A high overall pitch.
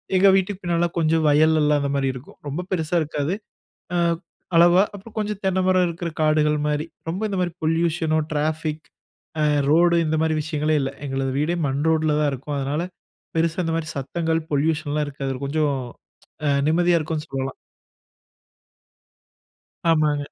No: medium, 155 Hz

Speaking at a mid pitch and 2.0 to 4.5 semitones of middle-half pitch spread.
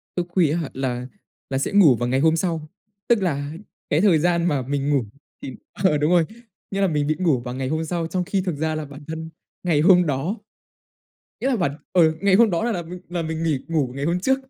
Yes: medium, 160 Hz; average, 3.8 semitones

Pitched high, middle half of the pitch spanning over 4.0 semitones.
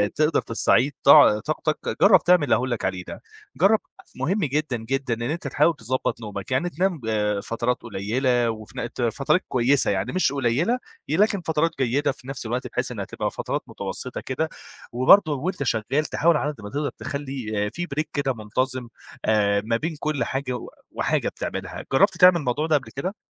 No: low, 135 Hz; average, 4.7 semitones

